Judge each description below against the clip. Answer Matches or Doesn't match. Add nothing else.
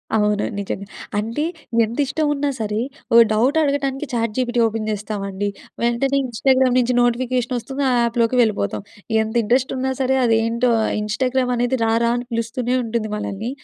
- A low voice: Doesn't match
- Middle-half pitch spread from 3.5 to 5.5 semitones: Doesn't match